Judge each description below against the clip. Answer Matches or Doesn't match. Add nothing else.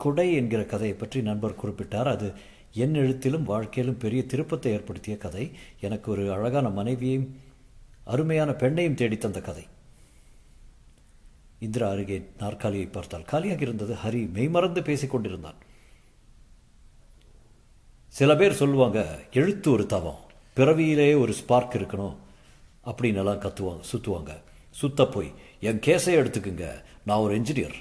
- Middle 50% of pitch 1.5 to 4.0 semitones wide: Doesn't match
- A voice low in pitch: Matches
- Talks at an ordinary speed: Matches